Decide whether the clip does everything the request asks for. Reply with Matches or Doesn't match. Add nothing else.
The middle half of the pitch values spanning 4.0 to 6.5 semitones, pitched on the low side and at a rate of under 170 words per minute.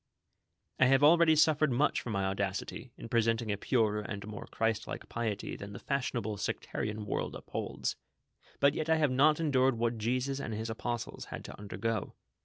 Doesn't match